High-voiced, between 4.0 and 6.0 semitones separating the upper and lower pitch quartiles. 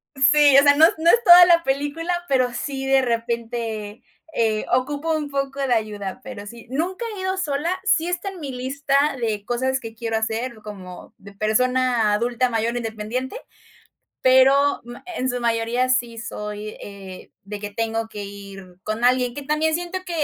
Yes: very high, 250 Hz; average, 4.3 semitones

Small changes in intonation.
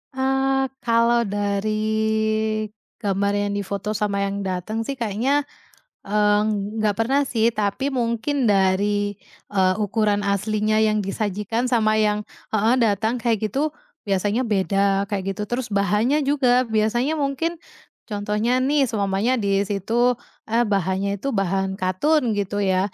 No: average, 3.2 semitones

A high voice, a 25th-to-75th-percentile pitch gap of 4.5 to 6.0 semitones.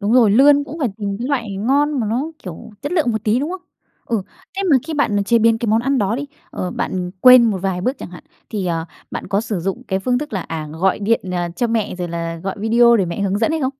Yes: high, 220 Hz; average, 4.8 semitones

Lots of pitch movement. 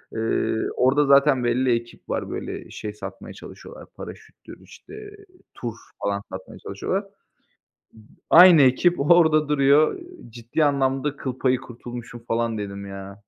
No: average, 4.3 semitones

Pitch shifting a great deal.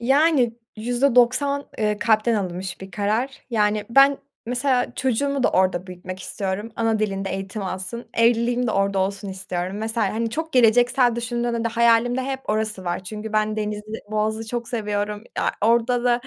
No: average, 3.0 semitones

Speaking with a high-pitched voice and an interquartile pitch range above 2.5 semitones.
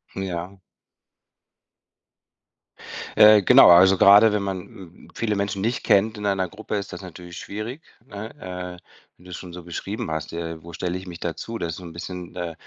No: very low, 95 Hz; average, 2.9 semitones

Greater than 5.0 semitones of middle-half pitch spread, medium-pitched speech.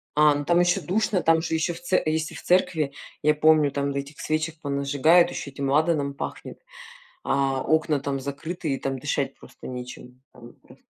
No: average, 2.7 semitones; medium, 150 Hz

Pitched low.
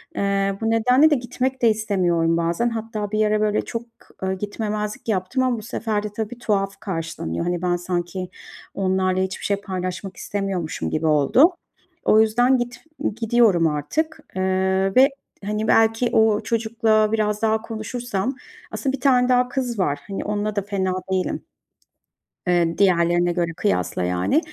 No: high, 210 Hz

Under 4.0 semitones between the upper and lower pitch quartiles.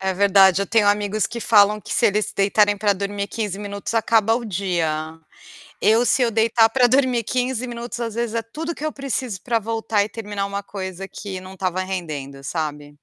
Yes: average, 3.2 semitones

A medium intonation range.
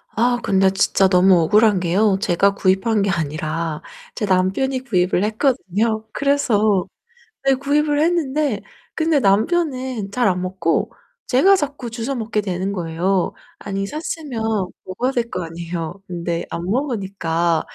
No: wide, 5.9 semitones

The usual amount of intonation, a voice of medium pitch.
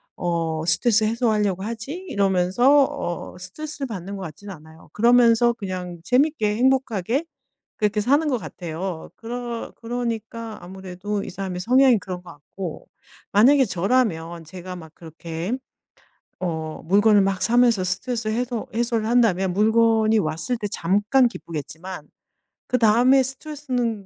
No: average, 4.9 semitones; high, 210 Hz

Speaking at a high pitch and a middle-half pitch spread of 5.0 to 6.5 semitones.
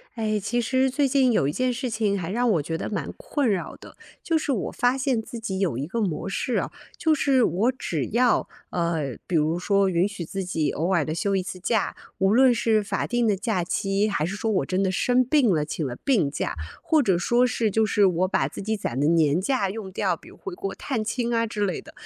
Yes: high, 205 Hz; wide, 5.4 semitones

